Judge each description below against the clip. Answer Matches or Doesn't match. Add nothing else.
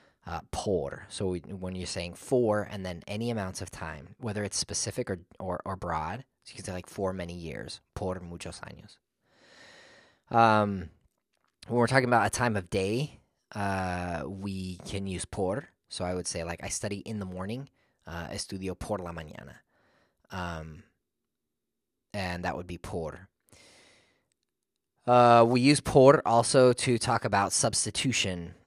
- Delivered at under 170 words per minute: Matches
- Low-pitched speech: Matches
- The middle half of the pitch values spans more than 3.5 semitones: Matches